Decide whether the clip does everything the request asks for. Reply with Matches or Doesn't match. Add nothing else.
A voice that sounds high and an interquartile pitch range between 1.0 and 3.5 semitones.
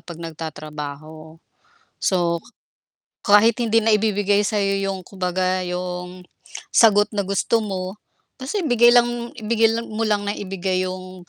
Matches